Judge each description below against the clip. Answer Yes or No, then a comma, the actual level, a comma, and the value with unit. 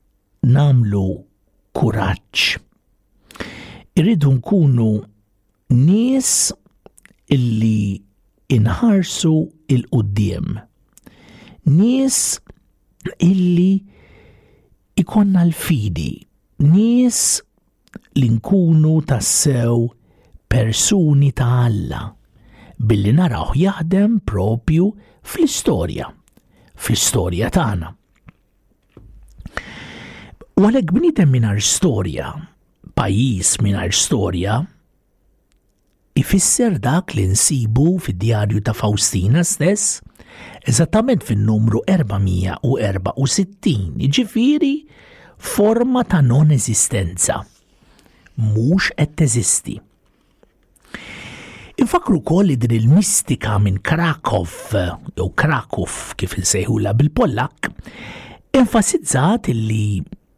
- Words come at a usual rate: No, slow, 70 wpm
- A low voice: Yes, low, 130 Hz